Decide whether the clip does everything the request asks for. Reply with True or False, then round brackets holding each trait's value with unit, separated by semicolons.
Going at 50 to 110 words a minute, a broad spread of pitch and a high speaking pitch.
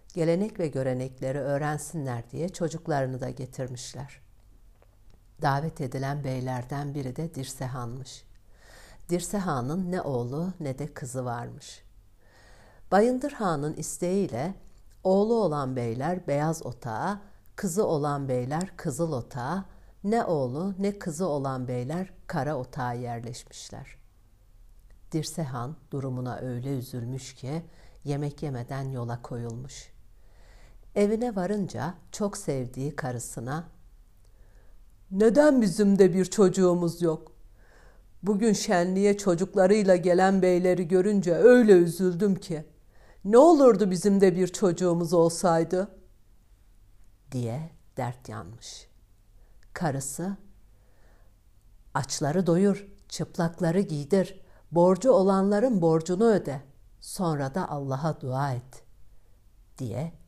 False (95 wpm; 7.2 semitones; 145 Hz)